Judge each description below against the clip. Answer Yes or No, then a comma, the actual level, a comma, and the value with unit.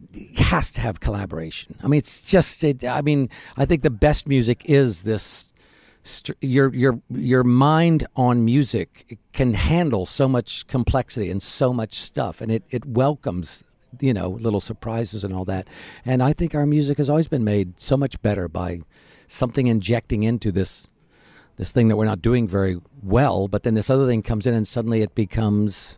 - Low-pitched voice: Yes, low, 120 Hz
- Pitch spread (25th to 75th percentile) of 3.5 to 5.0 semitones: Yes, average, 4.5 semitones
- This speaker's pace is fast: No, average, 185 wpm